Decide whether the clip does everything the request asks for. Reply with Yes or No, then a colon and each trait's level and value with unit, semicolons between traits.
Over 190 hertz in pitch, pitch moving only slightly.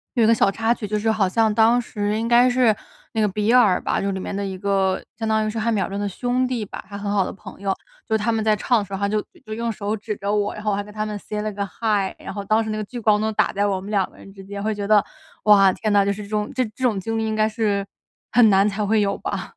Yes: high, 210 Hz; narrow, 1.6 semitones